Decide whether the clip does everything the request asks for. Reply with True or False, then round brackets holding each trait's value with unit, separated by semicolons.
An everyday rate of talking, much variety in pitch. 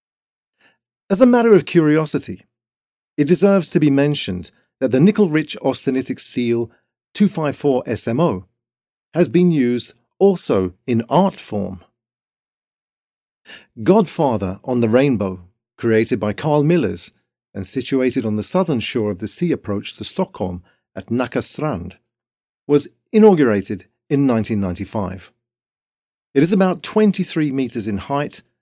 False (120 wpm; 6.6 semitones)